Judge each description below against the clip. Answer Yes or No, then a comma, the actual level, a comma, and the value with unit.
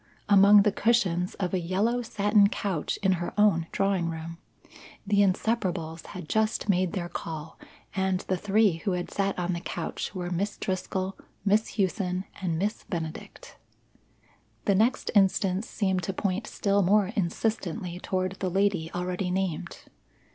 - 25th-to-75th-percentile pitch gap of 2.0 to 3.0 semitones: Yes, narrow, 2.4 semitones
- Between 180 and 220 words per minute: No, average, 150 wpm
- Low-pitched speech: No, high, 190 Hz